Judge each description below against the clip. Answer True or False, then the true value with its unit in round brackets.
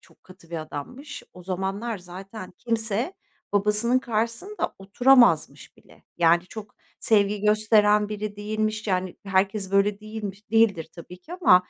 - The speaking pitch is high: True (210 Hz)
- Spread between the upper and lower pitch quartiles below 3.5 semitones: True (2.6 semitones)